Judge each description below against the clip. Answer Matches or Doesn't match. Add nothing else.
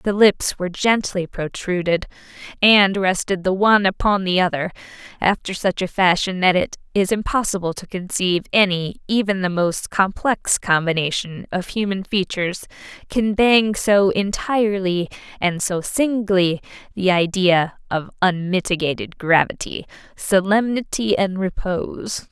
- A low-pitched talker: Doesn't match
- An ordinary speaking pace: Doesn't match